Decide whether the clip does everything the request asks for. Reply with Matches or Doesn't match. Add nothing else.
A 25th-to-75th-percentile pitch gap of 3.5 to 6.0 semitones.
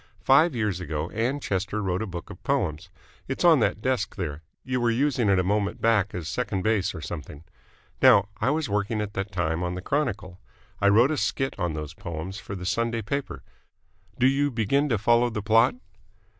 Matches